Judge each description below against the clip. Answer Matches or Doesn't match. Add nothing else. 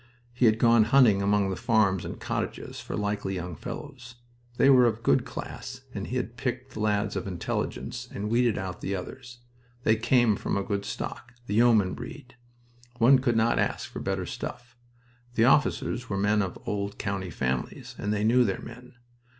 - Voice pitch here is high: Doesn't match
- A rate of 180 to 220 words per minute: Matches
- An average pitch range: Matches